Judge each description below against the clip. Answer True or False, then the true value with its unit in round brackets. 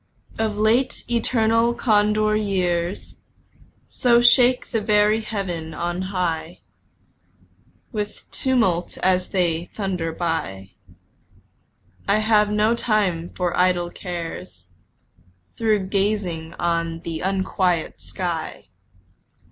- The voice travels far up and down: False (3.9 semitones)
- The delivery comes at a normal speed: False (95 wpm)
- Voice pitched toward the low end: False (190 Hz)